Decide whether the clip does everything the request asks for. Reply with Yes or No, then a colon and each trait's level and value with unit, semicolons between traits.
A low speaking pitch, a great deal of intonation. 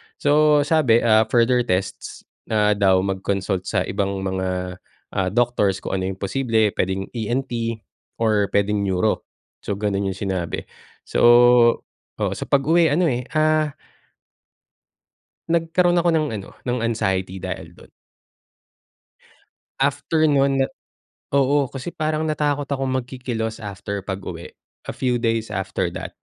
Yes: low, 115 Hz; wide, 6.4 semitones